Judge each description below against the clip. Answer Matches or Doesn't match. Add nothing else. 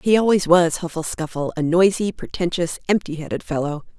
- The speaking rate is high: Doesn't match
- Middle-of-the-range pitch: Matches